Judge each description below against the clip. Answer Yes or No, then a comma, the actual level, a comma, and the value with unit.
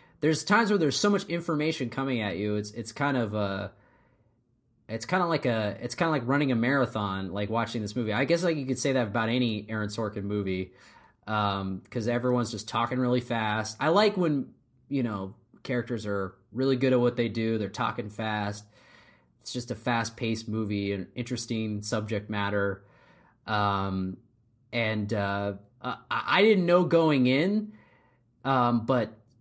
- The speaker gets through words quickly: No, average, 175 wpm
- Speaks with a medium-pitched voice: No, low, 120 Hz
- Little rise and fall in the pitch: No, average, 3.7 semitones